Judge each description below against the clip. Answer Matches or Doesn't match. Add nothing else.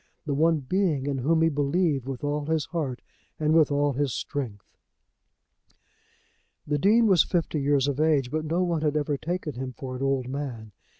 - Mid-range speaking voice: Matches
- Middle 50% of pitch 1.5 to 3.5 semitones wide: Matches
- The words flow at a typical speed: Matches